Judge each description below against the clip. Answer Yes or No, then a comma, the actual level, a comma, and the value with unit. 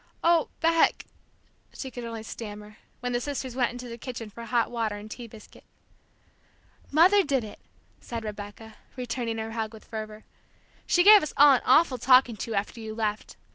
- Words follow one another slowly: No, average, 175 wpm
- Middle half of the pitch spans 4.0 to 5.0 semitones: No, average, 3.2 semitones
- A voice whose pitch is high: Yes, high, 235 Hz